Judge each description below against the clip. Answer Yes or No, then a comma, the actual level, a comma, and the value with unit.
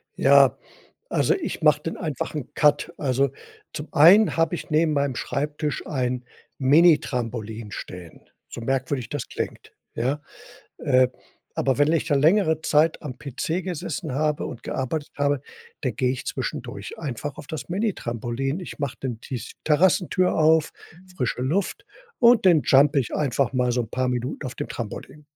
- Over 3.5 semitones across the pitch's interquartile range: Yes, average, 3.9 semitones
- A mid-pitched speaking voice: Yes, medium, 145 Hz